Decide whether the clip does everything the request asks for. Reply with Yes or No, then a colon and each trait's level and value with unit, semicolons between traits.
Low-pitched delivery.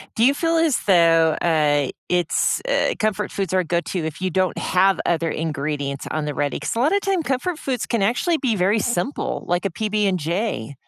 No: medium, 185 Hz